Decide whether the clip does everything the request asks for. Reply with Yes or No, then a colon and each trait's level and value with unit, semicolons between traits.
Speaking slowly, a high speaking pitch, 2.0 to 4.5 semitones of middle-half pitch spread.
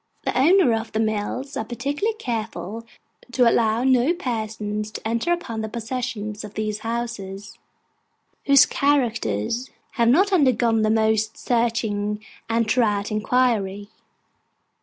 Yes: slow, 125 wpm; high, 230 Hz; average, 2.9 semitones